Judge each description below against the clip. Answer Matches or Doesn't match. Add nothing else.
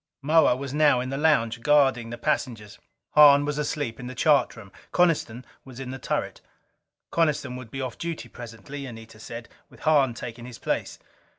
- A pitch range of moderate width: Matches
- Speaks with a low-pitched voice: Matches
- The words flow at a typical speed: Matches